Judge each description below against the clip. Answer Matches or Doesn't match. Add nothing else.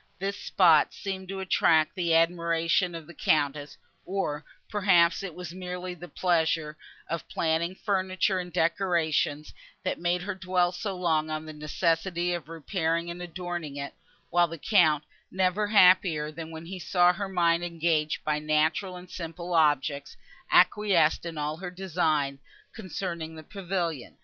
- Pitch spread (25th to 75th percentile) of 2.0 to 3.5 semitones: Matches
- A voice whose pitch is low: Doesn't match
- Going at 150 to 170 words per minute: Matches